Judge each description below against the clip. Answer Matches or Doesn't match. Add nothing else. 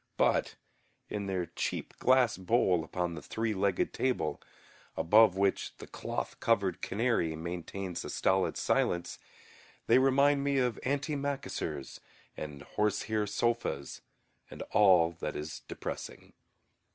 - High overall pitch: Doesn't match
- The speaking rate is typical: Doesn't match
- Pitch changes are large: Matches